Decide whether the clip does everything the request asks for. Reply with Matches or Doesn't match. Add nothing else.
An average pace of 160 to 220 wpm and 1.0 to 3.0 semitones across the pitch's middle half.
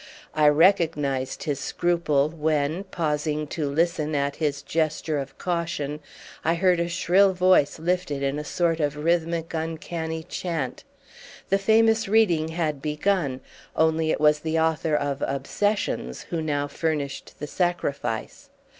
Doesn't match